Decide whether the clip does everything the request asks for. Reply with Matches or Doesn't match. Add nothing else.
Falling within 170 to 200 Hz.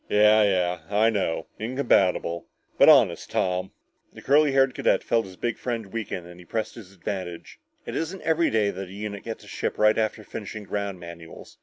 Doesn't match